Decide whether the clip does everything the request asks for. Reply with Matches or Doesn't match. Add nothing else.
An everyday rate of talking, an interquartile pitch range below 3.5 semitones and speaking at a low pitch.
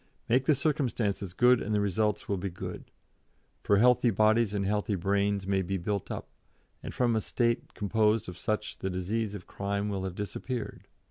Matches